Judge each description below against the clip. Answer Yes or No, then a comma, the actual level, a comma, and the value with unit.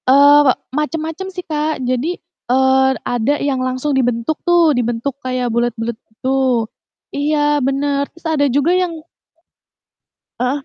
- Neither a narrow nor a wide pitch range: Yes, average, 3.3 semitones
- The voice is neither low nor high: No, very high, 280 Hz